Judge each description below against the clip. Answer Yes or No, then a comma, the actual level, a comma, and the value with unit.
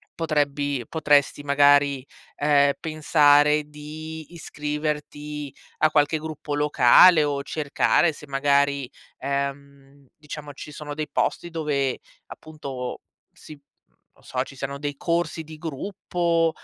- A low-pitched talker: No, medium, 145 Hz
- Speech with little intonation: Yes, narrow, 1.7 semitones